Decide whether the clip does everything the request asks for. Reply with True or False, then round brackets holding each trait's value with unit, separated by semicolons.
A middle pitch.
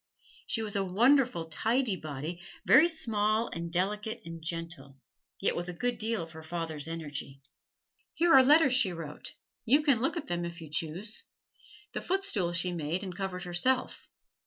True (180 Hz)